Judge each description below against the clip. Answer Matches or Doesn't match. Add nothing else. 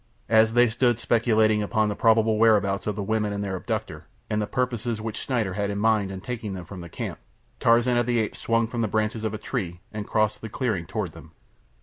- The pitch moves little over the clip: Matches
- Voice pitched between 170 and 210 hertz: Doesn't match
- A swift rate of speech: Matches